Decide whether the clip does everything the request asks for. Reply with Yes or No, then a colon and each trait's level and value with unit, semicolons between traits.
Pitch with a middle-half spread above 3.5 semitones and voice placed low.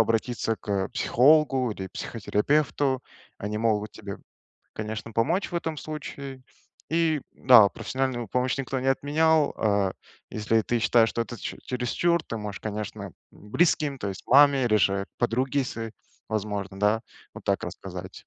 Yes: average, 4.6 semitones; low, 115 Hz